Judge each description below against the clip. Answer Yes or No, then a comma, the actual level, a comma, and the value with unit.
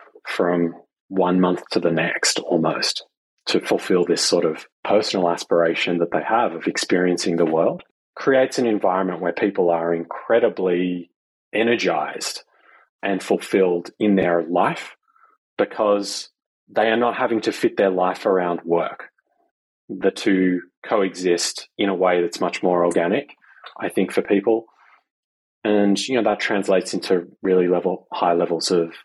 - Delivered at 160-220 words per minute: No, average, 145 wpm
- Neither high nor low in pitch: No, very low, 90 Hz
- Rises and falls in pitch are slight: Yes, narrow, 2.2 semitones